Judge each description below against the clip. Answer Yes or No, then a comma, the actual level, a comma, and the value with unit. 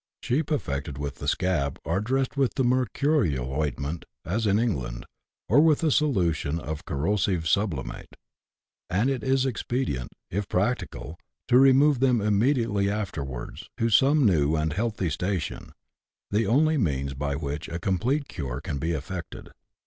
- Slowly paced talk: No, average, 150 wpm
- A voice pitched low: Yes, very low, 95 Hz